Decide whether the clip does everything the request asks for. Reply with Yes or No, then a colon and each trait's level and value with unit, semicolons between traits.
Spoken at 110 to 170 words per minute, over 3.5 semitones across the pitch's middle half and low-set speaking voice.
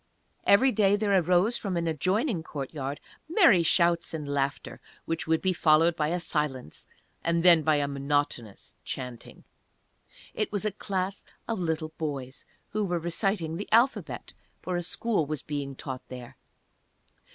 No: average, 150 wpm; average, 5.0 semitones; medium, 165 Hz